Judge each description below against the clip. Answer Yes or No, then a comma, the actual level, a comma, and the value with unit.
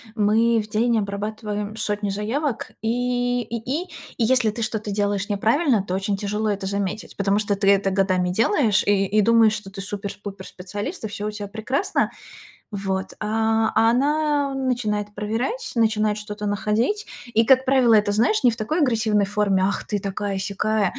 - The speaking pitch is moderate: No, high, 215 Hz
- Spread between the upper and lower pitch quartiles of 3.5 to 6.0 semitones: No, narrow, 2.5 semitones